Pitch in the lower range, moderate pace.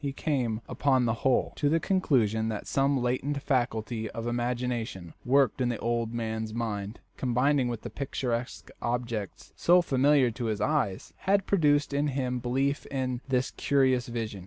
Yes: low, 125 Hz; average, 160 wpm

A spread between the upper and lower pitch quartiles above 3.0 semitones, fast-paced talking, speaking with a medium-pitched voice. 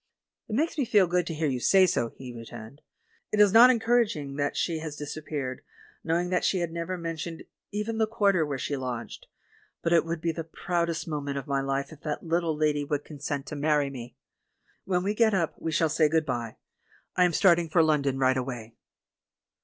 Yes: average, 4.1 semitones; fast, 210 wpm; medium, 160 Hz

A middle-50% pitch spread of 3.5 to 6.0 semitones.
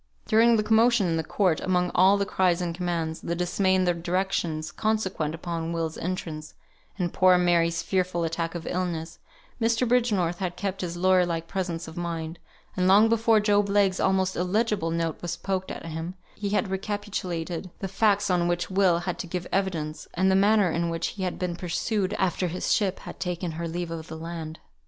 No: narrow, 2.6 semitones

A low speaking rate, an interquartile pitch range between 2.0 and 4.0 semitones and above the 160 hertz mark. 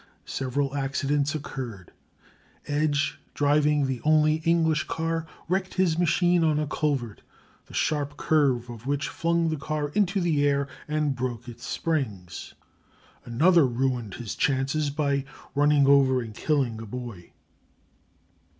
No: slow, 130 wpm; average, 3.3 semitones; medium, 145 Hz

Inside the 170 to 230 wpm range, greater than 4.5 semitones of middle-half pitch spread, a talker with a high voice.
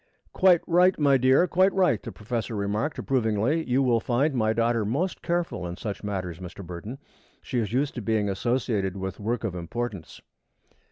No: average, 175 wpm; average, 5.1 semitones; low, 115 Hz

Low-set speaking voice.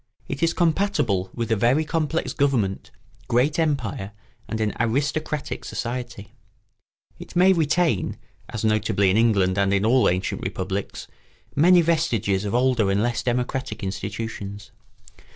Yes: low, 120 Hz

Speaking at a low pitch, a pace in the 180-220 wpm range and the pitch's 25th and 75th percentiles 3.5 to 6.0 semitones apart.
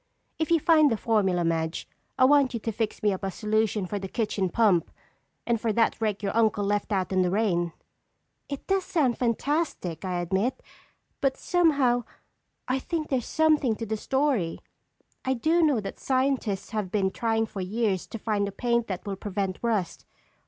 No: high, 220 Hz; average, 185 wpm; average, 5.0 semitones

